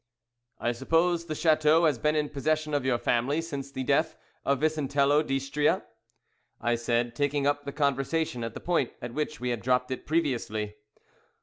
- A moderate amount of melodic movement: Yes, average, 3.5 semitones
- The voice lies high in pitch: No, medium, 140 Hz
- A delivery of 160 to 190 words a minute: Yes, average, 180 wpm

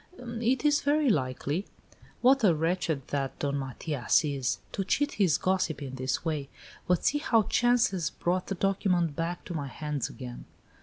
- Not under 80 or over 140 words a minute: No, average, 170 wpm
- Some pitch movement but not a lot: No, wide, 7.2 semitones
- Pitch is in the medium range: Yes, medium, 170 Hz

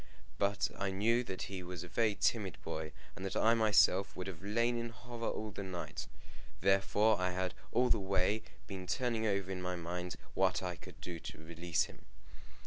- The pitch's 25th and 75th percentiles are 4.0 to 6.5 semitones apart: No, average, 3.4 semitones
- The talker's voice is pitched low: Yes, very low, 95 Hz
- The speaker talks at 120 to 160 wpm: No, average, 195 wpm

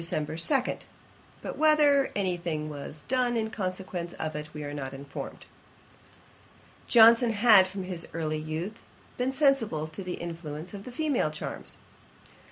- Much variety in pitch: Yes, wide, 6.8 semitones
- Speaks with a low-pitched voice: No, medium, 180 Hz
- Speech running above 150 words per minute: No, average, 140 wpm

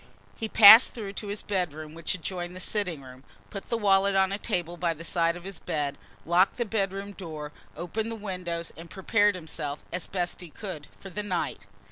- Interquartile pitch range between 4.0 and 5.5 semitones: No, average, 3.3 semitones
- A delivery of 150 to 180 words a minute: No, average, 200 wpm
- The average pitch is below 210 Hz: Yes, medium, 185 Hz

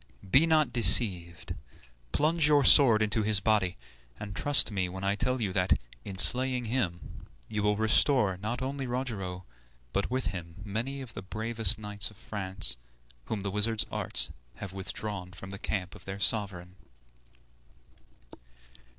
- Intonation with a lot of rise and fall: No, average, 4.2 semitones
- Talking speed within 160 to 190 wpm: No, average, 150 wpm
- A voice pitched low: Yes, low, 105 Hz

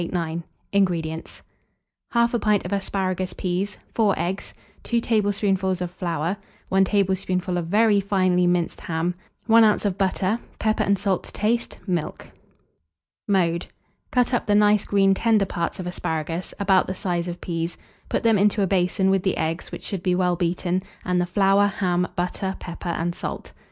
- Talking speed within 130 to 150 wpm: No, average, 165 wpm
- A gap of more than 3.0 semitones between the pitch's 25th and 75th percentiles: No, narrow, 2.4 semitones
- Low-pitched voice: No, high, 190 Hz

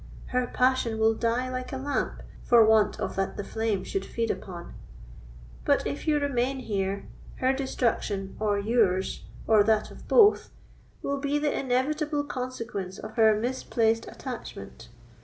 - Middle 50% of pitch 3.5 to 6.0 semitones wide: Yes, average, 3.9 semitones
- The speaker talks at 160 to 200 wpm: No, average, 150 wpm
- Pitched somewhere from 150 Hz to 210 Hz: No, high, 230 Hz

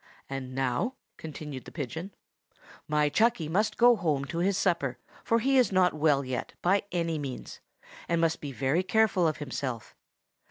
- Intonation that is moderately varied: No, wide, 5.7 semitones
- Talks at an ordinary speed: Yes, average, 165 wpm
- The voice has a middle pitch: Yes, medium, 160 Hz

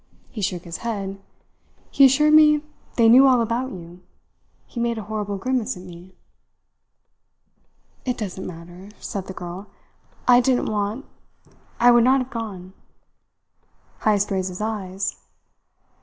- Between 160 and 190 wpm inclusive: No, average, 140 wpm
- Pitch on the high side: Yes, high, 210 Hz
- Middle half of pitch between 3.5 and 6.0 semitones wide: Yes, average, 4.6 semitones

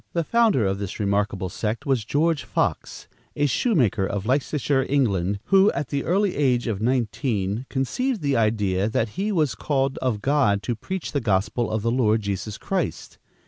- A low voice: Yes, low, 120 Hz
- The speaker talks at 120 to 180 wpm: Yes, average, 175 wpm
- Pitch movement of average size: No, wide, 5.7 semitones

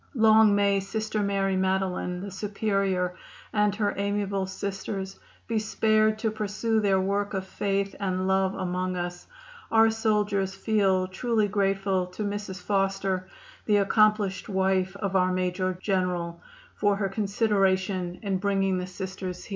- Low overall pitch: No, high, 195 Hz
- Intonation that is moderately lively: No, narrow, 1.7 semitones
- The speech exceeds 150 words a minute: No, average, 140 wpm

